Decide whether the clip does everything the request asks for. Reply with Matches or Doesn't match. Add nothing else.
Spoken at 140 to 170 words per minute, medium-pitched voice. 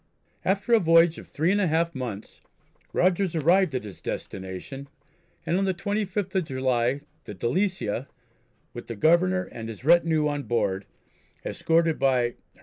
Matches